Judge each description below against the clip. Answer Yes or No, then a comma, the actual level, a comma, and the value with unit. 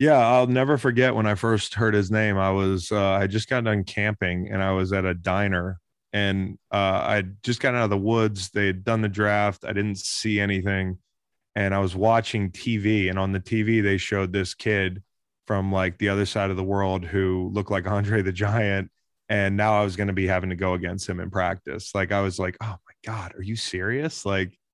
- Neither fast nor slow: No, fast, 230 wpm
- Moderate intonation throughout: No, narrow, 2.0 semitones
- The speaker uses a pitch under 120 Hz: Yes, low, 100 Hz